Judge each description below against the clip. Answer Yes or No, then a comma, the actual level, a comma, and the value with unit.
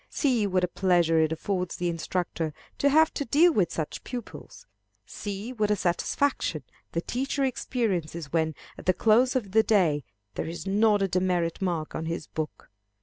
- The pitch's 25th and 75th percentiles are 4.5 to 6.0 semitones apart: Yes, average, 5.2 semitones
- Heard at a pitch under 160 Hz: No, medium, 185 Hz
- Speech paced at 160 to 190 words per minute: Yes, average, 175 wpm